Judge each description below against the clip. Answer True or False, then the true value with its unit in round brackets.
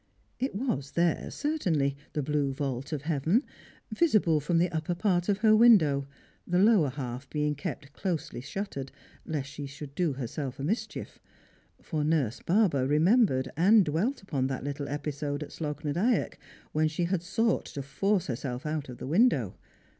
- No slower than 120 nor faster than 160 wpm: False (175 wpm)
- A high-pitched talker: False (155 Hz)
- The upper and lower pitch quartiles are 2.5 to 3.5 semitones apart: False (5.3 semitones)